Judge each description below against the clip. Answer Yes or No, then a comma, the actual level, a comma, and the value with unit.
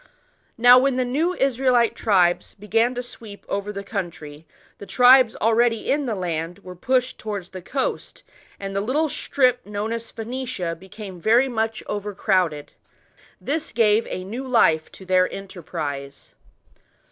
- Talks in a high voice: Yes, high, 215 Hz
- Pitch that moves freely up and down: No, average, 5.0 semitones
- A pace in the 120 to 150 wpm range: Yes, average, 145 wpm